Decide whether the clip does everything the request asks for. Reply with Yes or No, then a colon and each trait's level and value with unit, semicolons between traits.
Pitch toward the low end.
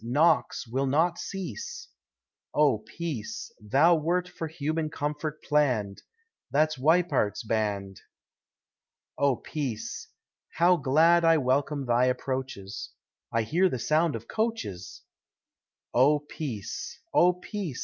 No: medium, 145 Hz